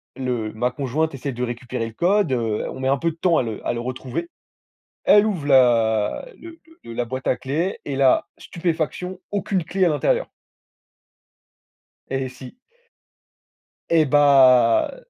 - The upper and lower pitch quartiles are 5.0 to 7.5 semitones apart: Yes, average, 5.3 semitones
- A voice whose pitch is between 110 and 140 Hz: Yes, low, 135 Hz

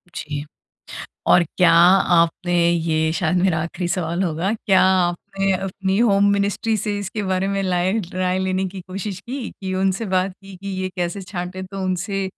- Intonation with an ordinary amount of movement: No, narrow, 1.9 semitones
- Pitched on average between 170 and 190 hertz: Yes, medium, 185 Hz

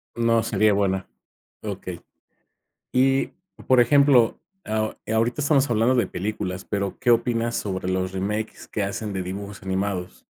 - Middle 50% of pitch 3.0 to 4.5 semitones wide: Yes, average, 3.6 semitones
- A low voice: Yes, low, 110 Hz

